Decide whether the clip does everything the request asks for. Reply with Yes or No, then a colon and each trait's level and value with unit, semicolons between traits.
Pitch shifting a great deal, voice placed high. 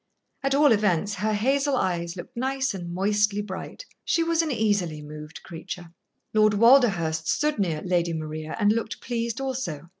Yes: wide, 6.7 semitones; high, 205 Hz